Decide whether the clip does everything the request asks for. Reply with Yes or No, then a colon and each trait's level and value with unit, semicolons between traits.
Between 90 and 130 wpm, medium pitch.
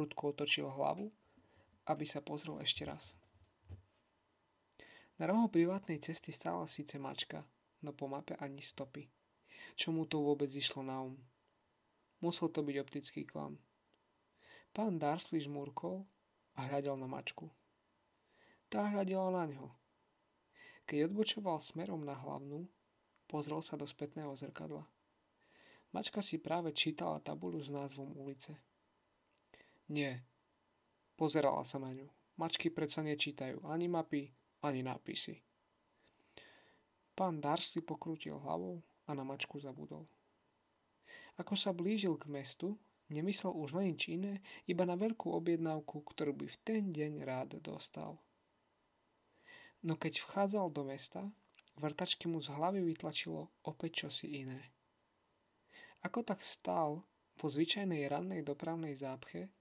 Yes: average, 125 wpm; medium, 150 Hz